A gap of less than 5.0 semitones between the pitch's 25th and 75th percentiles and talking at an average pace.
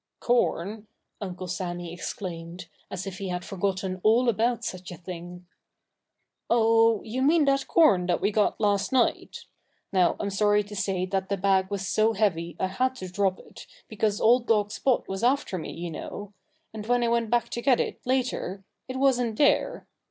Yes: average, 4.2 semitones; average, 180 wpm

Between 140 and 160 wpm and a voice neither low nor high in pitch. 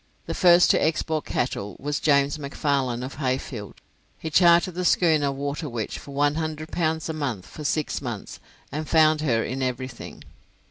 Yes: average, 155 wpm; medium, 145 Hz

